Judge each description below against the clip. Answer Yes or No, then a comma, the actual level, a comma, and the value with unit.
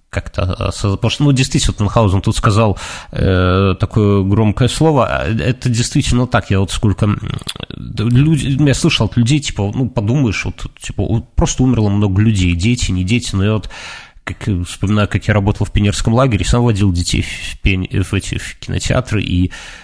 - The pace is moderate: No, fast, 170 wpm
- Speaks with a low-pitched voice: Yes, low, 105 Hz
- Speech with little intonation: No, average, 3.6 semitones